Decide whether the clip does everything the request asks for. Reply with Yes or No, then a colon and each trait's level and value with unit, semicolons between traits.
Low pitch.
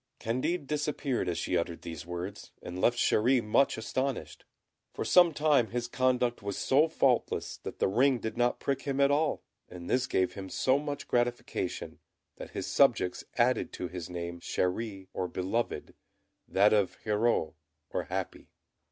Yes: low, 120 Hz